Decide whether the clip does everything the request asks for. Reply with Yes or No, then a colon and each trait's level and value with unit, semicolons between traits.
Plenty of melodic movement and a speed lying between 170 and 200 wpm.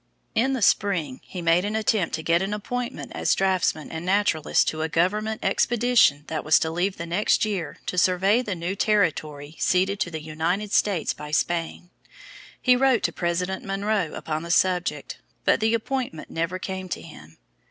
No: average, 4.3 semitones; average, 180 wpm